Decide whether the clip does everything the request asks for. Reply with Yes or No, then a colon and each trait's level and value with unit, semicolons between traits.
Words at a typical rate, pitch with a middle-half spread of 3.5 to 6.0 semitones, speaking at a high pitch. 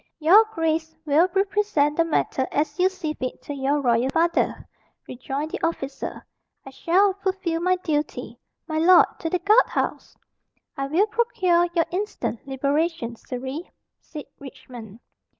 Yes: average, 145 wpm; average, 4.8 semitones; very high, 320 Hz